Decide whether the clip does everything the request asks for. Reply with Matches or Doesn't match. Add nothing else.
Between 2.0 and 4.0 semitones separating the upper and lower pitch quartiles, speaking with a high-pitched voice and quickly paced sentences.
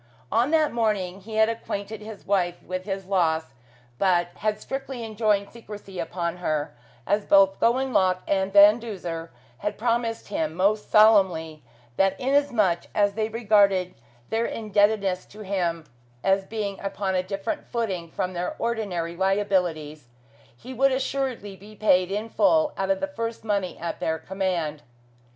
Doesn't match